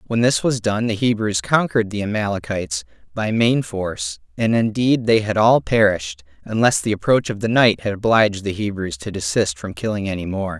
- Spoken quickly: No, average, 195 wpm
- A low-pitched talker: Yes, low, 105 Hz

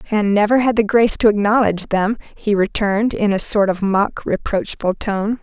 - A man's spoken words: No, female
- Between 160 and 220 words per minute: Yes, average, 190 wpm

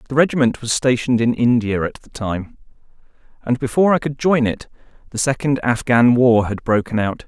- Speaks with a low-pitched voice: Yes, low, 125 Hz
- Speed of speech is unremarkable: Yes, average, 180 wpm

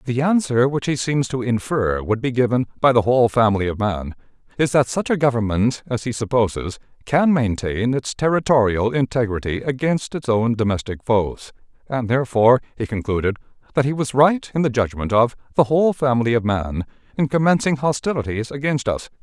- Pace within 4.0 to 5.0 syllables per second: No, 5.5 syllables/s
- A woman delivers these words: No, male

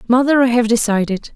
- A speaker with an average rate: Yes, average, 180 wpm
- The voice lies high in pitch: Yes, high, 235 Hz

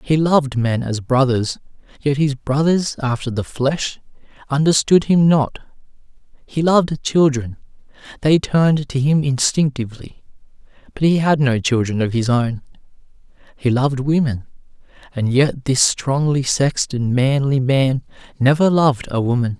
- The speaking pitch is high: No, low, 135 Hz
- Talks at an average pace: No, slow, 130 wpm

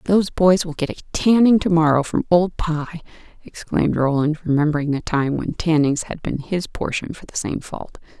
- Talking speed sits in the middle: Yes, average, 190 wpm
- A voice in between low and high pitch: Yes, medium, 160 Hz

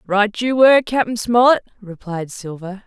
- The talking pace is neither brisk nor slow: Yes, average, 145 wpm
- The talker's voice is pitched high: Yes, high, 215 Hz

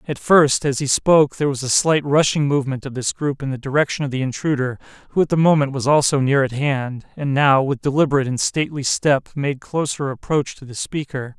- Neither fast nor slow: No, fast, 220 wpm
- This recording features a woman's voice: No, male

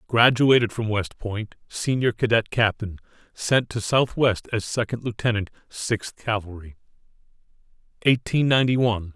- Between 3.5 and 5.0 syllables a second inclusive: Yes, 4.7 syllables/s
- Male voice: Yes, male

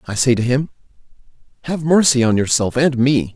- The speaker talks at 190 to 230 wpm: No, average, 180 wpm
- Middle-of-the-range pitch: No, low, 130 Hz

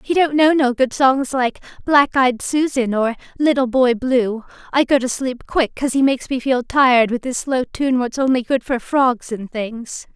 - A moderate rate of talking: No, fast, 215 wpm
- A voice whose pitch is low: No, very high, 255 Hz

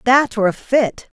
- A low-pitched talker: No, high, 235 Hz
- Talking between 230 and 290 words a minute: No, average, 200 wpm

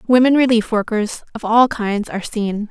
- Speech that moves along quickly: No, average, 180 wpm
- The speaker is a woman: Yes, female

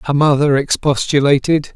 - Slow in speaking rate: Yes, slow, 105 wpm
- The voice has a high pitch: No, medium, 145 Hz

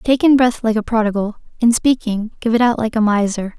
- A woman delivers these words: Yes, female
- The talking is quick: Yes, fast, 235 wpm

